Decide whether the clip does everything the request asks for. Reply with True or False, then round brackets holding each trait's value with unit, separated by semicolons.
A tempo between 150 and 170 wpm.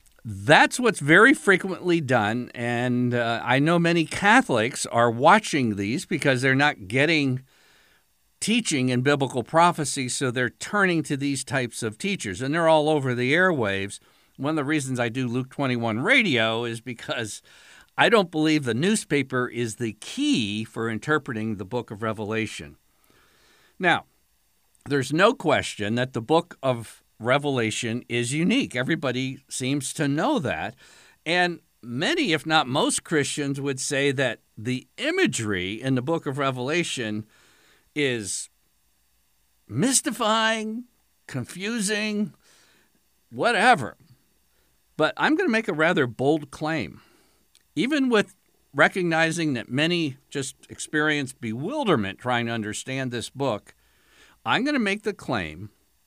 False (135 wpm)